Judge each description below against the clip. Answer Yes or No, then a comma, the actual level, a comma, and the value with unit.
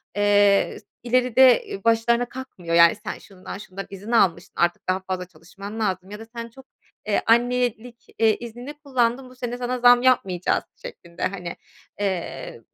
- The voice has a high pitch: Yes, high, 220 Hz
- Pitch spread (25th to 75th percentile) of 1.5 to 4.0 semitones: No, average, 4.5 semitones